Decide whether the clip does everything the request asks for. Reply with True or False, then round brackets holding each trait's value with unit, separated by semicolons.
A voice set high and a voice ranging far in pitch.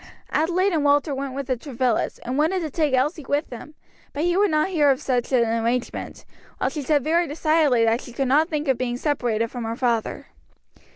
False (280 Hz; 3.9 semitones)